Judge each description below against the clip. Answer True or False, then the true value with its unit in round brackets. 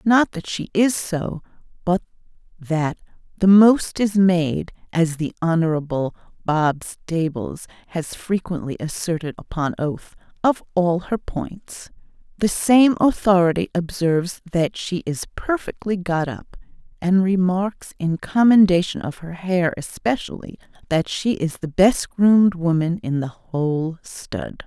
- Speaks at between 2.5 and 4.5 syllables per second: True (4.0 syllables/s)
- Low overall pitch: False (175 Hz)